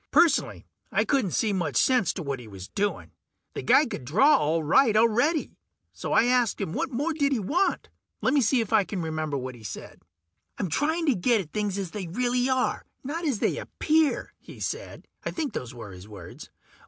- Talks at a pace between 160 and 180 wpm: No, fast, 205 wpm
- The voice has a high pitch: Yes, high, 215 Hz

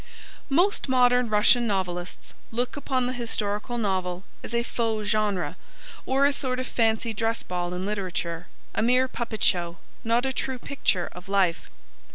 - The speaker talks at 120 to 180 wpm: Yes, average, 160 wpm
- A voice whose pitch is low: No, high, 225 Hz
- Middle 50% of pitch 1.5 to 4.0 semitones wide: No, average, 4.8 semitones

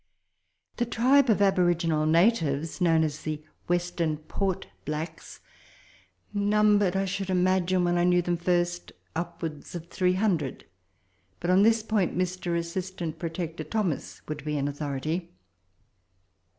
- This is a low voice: No, medium, 175 Hz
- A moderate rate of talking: No, slow, 125 wpm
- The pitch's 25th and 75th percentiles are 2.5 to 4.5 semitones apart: Yes, average, 2.9 semitones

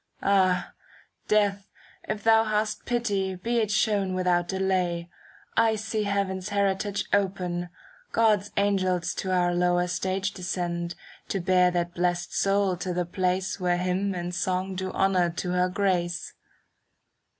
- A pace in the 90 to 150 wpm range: Yes, average, 140 wpm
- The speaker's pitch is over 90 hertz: Yes, medium, 185 Hz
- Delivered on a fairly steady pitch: Yes, narrow, 2.1 semitones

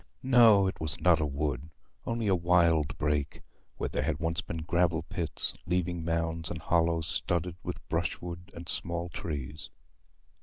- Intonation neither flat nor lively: No, narrow, 1.8 semitones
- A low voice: Yes, very low, 85 Hz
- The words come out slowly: No, average, 155 wpm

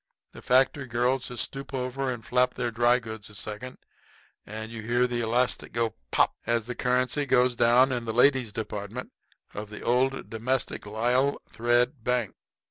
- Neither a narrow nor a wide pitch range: No, narrow, 2.1 semitones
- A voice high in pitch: No, low, 120 Hz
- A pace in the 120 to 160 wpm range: No, average, 170 wpm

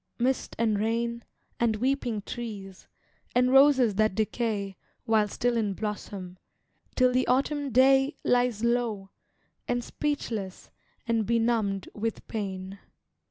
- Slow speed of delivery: Yes, slow, 115 wpm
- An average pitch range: Yes, average, 3.2 semitones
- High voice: Yes, high, 230 Hz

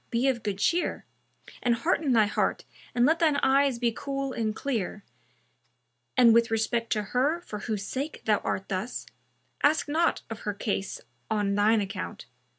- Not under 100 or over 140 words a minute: No, average, 165 wpm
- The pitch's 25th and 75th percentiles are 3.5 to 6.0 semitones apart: Yes, average, 4.6 semitones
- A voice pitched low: No, high, 230 Hz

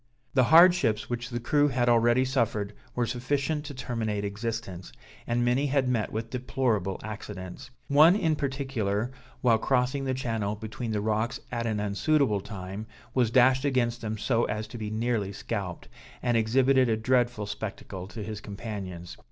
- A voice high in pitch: No, low, 115 Hz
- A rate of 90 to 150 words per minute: No, average, 160 wpm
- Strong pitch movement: No, average, 3.5 semitones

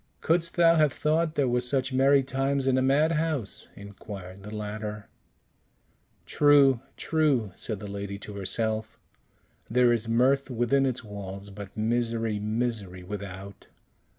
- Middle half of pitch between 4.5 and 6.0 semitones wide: Yes, average, 5.0 semitones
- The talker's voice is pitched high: No, low, 115 Hz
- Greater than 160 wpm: No, slow, 135 wpm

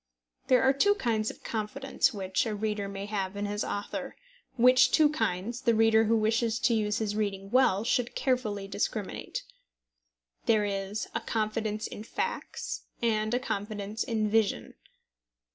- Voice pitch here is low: No, high, 215 Hz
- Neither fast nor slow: Yes, average, 155 wpm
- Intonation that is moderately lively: No, narrow, 2.3 semitones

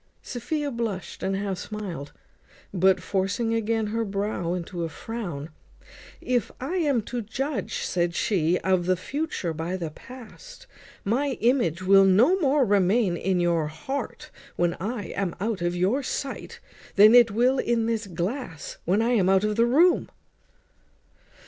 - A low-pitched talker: No, high, 205 Hz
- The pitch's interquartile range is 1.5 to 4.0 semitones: No, average, 5.1 semitones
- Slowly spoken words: No, average, 155 wpm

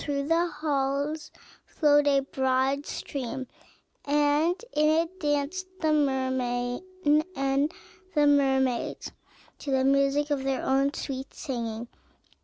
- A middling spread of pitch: No, narrow, 2.0 semitones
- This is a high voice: Yes, very high, 280 Hz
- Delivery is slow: Yes, slow, 115 wpm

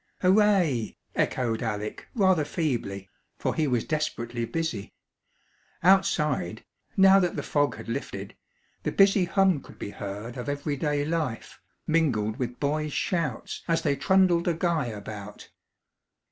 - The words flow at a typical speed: No, slow, 130 wpm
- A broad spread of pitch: Yes, wide, 6.7 semitones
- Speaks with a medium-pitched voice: Yes, medium, 145 Hz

